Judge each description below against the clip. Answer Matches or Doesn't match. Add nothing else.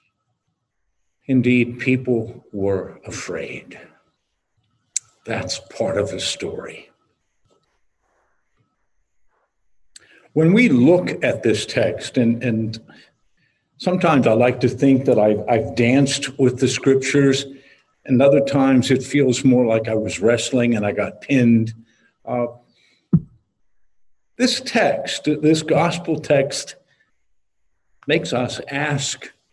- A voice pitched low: Matches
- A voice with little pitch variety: Doesn't match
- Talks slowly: Matches